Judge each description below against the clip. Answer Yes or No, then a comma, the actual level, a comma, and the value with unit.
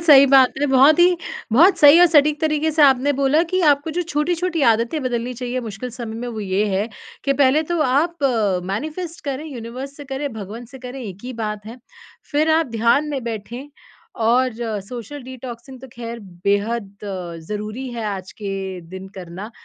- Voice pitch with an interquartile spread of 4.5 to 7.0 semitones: Yes, average, 4.8 semitones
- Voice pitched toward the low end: No, very high, 255 Hz